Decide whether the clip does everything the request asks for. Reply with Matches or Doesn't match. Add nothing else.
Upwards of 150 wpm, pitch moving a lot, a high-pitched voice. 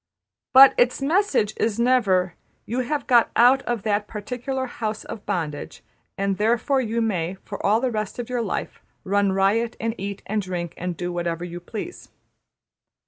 Doesn't match